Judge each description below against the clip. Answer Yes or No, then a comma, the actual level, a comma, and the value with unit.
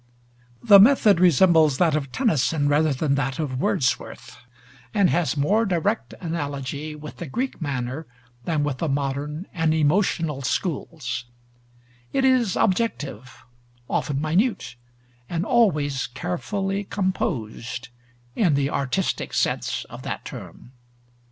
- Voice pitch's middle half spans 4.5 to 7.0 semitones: Yes, average, 5.2 semitones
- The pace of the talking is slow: Yes, slow, 120 wpm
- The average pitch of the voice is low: No, medium, 155 Hz